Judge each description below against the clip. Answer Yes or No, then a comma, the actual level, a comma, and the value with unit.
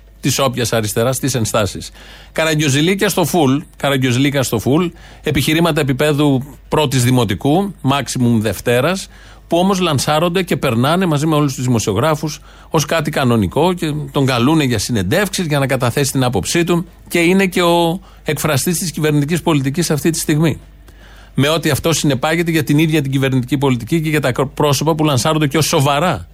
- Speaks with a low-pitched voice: No, medium, 150 Hz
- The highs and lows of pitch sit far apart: No, average, 4.0 semitones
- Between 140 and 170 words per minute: Yes, average, 160 wpm